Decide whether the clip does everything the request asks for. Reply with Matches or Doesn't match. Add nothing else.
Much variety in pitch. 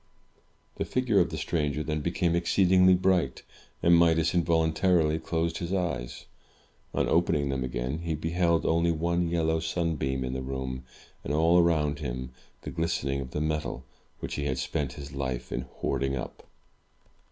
Doesn't match